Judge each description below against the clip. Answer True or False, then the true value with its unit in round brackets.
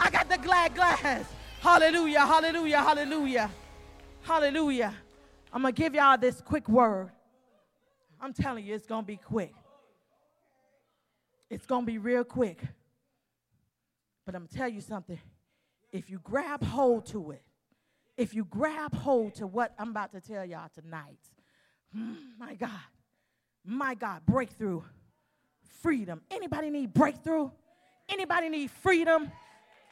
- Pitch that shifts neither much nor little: False (6.7 semitones)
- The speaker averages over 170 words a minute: False (135 wpm)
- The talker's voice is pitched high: True (245 Hz)